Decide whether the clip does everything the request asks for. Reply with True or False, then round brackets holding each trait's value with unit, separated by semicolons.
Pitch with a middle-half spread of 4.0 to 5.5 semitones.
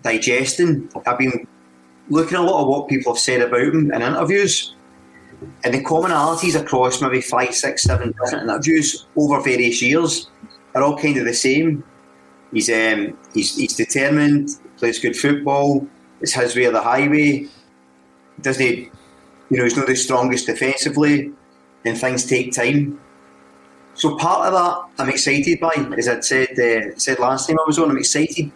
True (4.5 semitones)